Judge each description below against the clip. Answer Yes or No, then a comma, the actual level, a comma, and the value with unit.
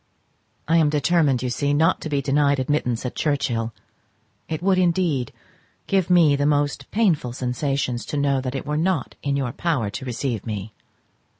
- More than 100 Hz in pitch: Yes, medium, 140 Hz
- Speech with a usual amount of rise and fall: Yes, average, 3.9 semitones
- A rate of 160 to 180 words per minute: Yes, average, 170 wpm